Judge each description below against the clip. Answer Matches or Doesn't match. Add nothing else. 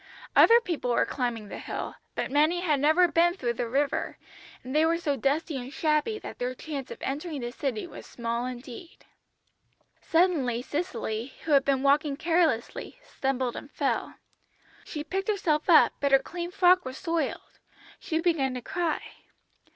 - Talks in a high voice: Matches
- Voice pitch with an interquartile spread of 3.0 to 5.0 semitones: Matches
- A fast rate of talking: Doesn't match